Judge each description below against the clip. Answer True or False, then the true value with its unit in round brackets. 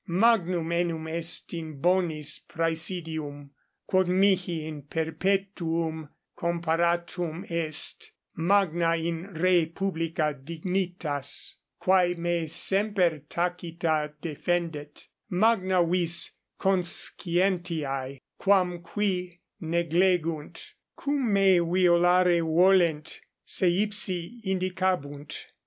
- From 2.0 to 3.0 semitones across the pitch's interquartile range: True (2.4 semitones)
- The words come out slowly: True (80 wpm)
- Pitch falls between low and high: True (170 Hz)